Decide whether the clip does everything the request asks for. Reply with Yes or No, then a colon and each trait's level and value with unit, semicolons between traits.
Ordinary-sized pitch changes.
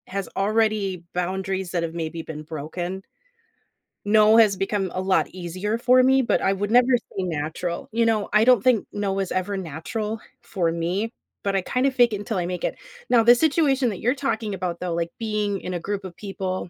Yes: average, 3.8 semitones